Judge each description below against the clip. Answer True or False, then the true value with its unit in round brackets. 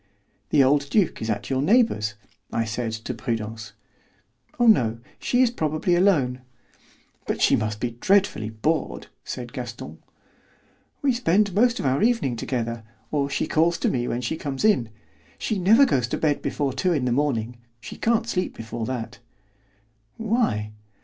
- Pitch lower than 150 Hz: True (135 Hz)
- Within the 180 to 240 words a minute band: False (165 wpm)